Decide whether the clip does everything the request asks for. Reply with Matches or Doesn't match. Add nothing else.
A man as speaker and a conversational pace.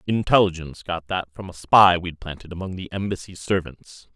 Matches